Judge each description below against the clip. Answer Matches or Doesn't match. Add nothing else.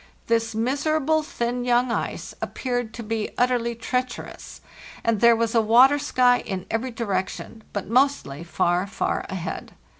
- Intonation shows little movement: Matches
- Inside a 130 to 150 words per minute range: Matches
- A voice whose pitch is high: Matches